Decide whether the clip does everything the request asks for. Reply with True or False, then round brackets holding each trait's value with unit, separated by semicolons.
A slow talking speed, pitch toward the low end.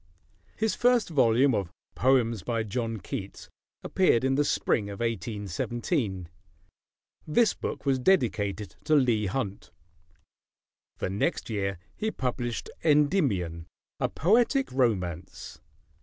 True (110 wpm; 120 Hz)